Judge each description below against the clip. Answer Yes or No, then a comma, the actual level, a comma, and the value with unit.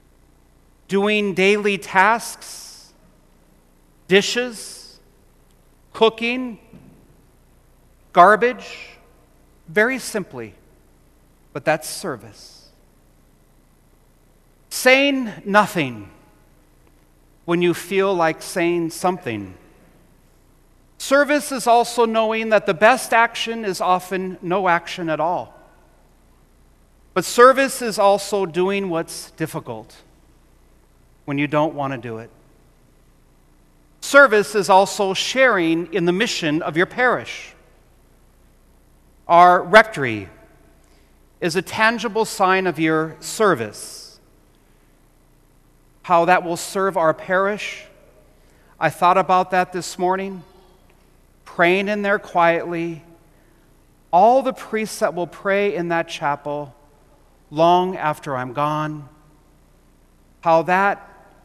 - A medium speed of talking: No, slow, 95 wpm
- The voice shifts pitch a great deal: No, average, 4.7 semitones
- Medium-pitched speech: Yes, medium, 180 Hz